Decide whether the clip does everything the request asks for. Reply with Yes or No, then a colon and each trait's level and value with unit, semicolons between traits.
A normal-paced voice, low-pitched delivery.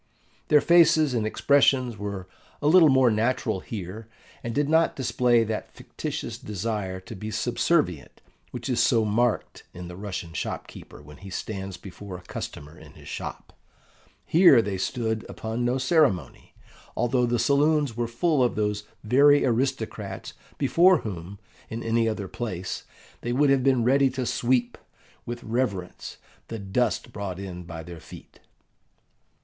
Yes: average, 155 wpm; low, 115 Hz